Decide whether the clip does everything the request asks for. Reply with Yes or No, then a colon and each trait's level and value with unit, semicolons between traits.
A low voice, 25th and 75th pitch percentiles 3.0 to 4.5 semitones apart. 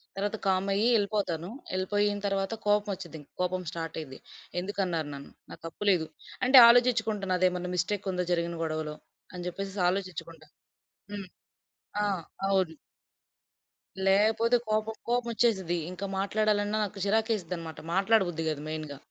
No: high, 195 Hz; average, 3.4 semitones